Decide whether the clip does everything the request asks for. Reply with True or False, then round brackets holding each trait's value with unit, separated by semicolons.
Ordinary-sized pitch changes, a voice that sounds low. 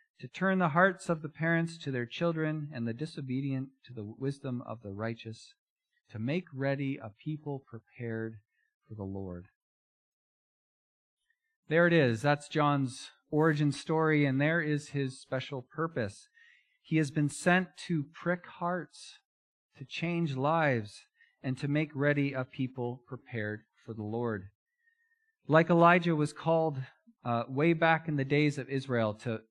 False (4.9 semitones; 145 Hz)